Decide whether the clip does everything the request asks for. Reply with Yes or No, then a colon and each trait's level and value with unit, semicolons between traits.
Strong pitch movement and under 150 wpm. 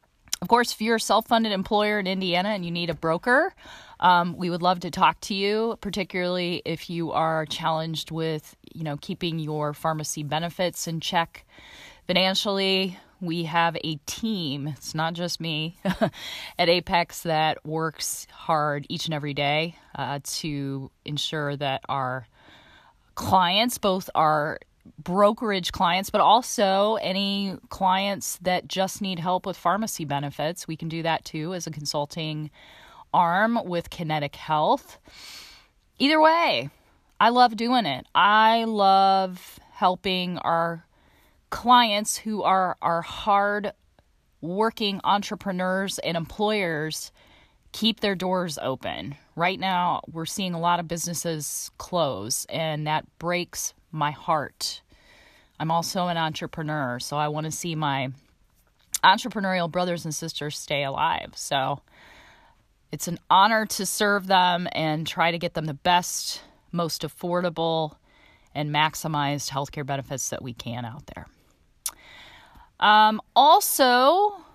No: average, 4.1 semitones; slow, 135 wpm